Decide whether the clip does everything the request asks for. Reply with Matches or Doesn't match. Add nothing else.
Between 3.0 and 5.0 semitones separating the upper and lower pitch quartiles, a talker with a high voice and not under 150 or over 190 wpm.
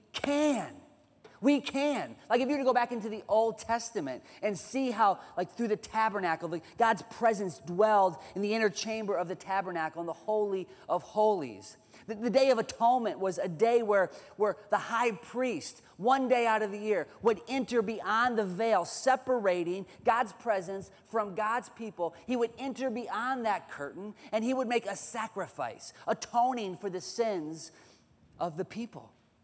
Matches